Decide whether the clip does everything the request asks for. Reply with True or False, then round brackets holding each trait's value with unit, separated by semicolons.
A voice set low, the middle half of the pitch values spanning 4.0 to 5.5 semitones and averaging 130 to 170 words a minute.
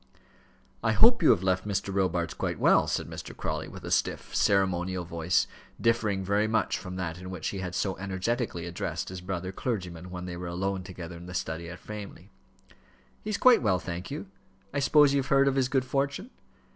False (95 Hz; 4.5 semitones; 205 wpm)